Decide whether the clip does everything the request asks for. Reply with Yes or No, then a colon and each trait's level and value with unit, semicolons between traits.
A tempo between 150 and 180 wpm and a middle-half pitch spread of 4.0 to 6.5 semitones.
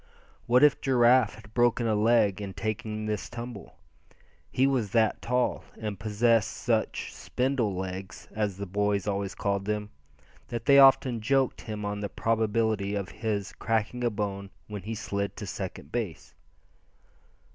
No: average, 155 wpm; average, 2.9 semitones